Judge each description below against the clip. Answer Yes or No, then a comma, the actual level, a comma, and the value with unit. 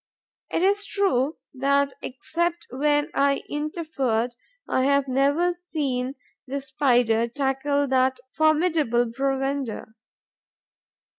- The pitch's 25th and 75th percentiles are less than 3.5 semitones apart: Yes, average, 3.0 semitones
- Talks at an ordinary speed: No, slow, 95 wpm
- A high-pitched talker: Yes, very high, 275 Hz